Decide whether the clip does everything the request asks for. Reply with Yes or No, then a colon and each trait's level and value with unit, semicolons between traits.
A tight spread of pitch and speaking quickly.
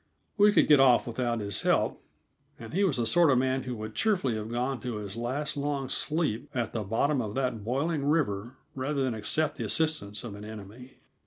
No: average, 4.5 semitones; fast, 210 wpm